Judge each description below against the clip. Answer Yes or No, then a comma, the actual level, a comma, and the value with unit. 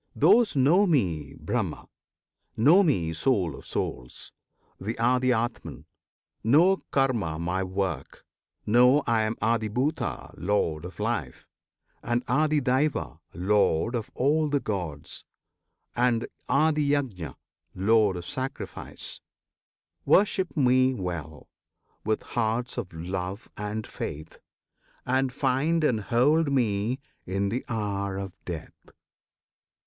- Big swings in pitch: Yes, wide, 5.9 semitones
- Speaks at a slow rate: Yes, slow, 105 wpm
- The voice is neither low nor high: No, low, 115 Hz